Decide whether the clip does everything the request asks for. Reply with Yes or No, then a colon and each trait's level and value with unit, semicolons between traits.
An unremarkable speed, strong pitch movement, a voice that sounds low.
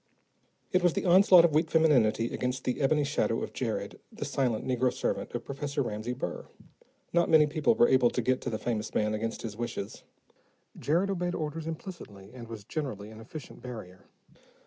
Yes: average, 185 wpm; wide, 5.9 semitones; low, 130 Hz